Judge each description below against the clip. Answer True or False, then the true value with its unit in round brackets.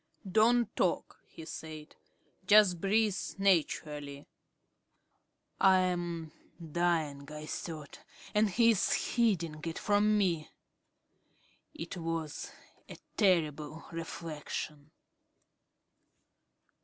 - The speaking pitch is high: False (170 Hz)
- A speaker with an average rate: False (85 wpm)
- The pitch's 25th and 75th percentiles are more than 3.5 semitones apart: True (4.3 semitones)